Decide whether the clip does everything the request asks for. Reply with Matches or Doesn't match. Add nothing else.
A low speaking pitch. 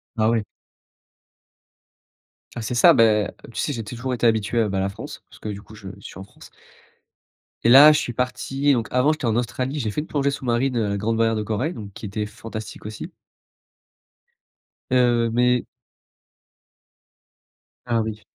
Matches